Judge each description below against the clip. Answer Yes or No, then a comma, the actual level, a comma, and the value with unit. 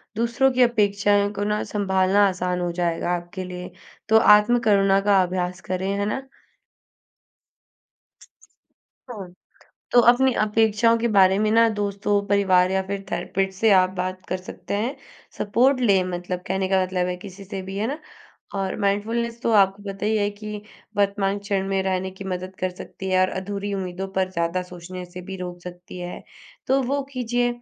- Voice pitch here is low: No, high, 195 Hz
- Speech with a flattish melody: Yes, narrow, 2.3 semitones